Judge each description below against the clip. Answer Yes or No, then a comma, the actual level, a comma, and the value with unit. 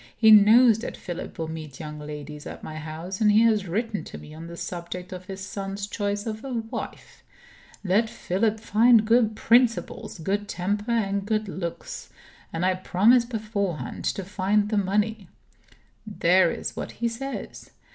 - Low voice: No, high, 205 Hz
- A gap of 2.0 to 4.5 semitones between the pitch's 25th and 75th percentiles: Yes, average, 3.5 semitones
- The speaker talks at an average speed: Yes, average, 165 wpm